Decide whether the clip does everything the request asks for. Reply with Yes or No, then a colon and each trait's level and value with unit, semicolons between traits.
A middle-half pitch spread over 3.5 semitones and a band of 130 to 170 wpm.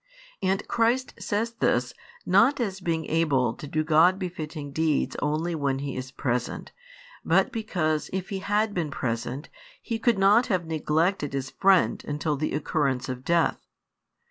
Yes: average, 5.3 semitones; average, 155 wpm